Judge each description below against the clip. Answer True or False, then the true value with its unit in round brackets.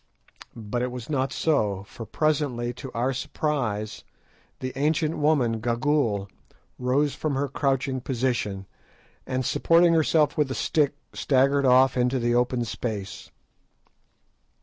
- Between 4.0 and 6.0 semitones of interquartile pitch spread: False (3.3 semitones)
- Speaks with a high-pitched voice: False (130 Hz)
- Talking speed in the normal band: False (125 wpm)